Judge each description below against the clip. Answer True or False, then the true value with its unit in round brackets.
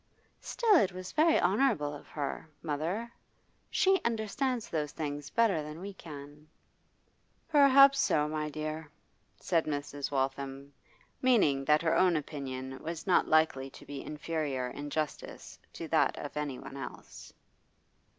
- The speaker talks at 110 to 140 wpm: True (135 wpm)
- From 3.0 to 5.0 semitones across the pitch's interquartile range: False (5.5 semitones)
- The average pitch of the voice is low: False (155 Hz)